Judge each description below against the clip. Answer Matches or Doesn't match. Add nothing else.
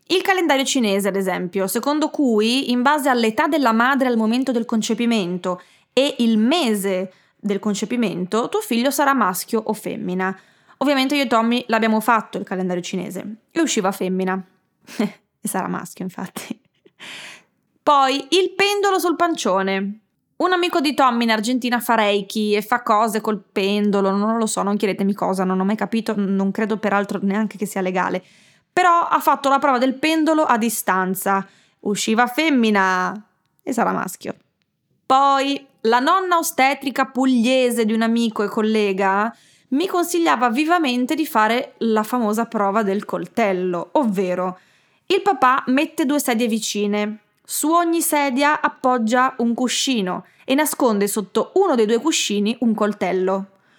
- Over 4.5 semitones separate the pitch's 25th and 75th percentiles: Matches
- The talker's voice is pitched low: Doesn't match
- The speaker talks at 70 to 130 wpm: Doesn't match